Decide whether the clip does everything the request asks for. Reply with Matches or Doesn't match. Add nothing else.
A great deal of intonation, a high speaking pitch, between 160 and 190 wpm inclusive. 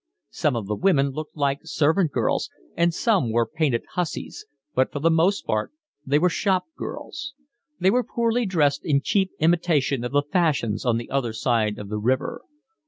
Doesn't match